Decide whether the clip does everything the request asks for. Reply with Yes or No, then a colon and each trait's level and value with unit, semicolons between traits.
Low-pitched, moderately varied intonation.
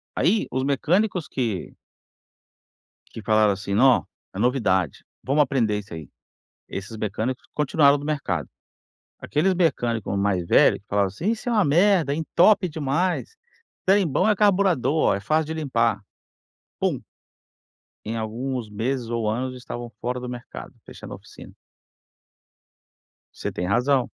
No: low, 130 Hz; wide, 6.4 semitones